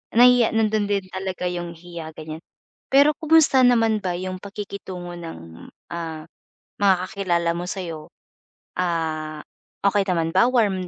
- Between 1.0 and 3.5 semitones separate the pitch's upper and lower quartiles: No, average, 3.9 semitones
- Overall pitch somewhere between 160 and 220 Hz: Yes, medium, 185 Hz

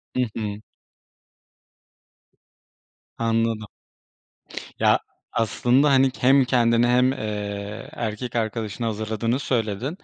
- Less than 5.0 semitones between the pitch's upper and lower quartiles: Yes, average, 2.8 semitones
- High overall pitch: No, low, 115 Hz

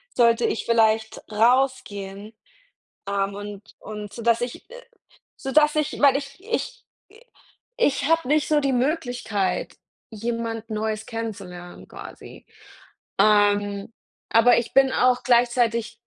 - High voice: Yes, high, 235 Hz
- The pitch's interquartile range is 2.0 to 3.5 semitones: No, average, 4.1 semitones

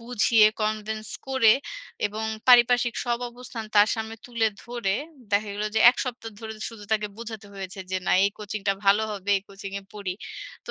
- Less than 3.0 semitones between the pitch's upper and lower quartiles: Yes, narrow, 2.4 semitones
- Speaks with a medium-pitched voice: No, high, 220 Hz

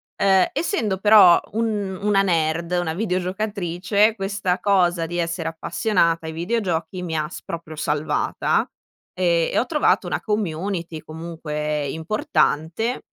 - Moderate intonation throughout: Yes, average, 3.7 semitones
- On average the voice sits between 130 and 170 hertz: No, medium, 180 Hz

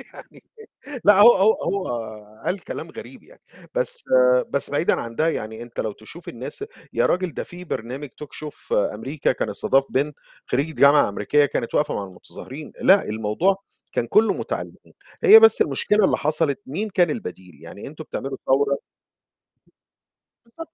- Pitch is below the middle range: No, medium, 150 Hz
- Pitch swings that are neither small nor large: No, wide, 8.0 semitones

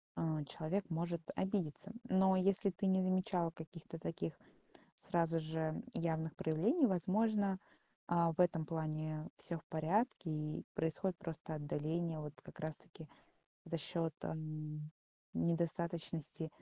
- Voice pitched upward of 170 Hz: No, medium, 165 Hz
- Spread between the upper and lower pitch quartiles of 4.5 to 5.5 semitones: No, average, 2.9 semitones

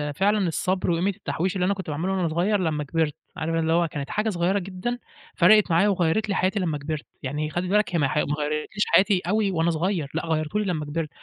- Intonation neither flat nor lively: Yes, average, 3.7 semitones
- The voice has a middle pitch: Yes, medium, 175 Hz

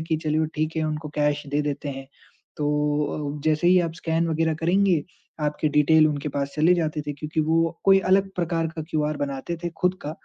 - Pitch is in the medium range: Yes, medium, 155 Hz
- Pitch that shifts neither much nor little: No, narrow, 1.9 semitones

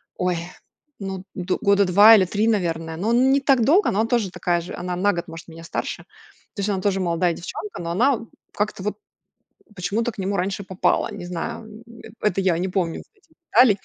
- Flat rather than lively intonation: No, average, 3.5 semitones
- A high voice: Yes, high, 195 Hz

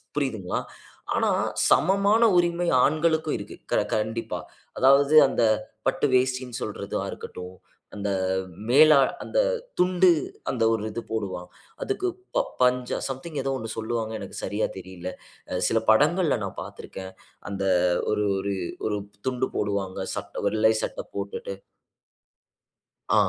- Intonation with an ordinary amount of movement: No, wide, 6.6 semitones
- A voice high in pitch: No, low, 120 Hz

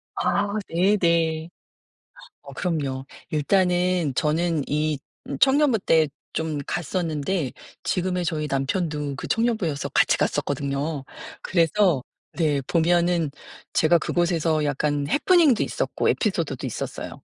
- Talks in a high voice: No, medium, 165 Hz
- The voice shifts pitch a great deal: No, average, 3.5 semitones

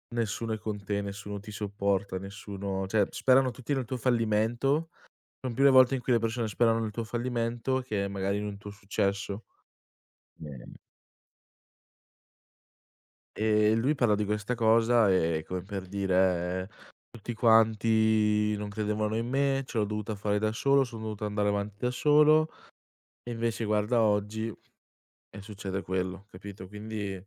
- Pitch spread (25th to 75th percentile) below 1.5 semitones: No, narrow, 2.5 semitones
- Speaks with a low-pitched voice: Yes, low, 105 Hz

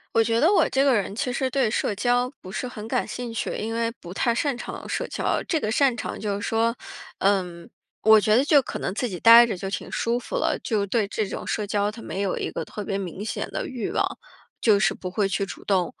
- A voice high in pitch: Yes, high, 225 Hz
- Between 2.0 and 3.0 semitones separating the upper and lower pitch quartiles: No, average, 3.5 semitones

